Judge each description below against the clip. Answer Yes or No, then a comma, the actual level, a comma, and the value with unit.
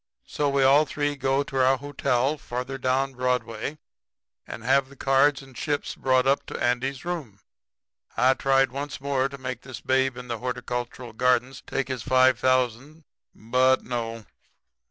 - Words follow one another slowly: No, average, 160 wpm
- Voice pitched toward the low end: Yes, low, 130 Hz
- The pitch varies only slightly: Yes, narrow, 1.6 semitones